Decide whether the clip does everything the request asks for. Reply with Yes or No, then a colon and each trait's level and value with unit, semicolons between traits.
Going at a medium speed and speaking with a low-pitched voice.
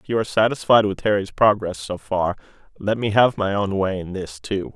No: fast, 225 wpm; low, 100 Hz